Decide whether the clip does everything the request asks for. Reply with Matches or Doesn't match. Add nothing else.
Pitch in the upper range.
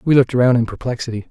Doesn't match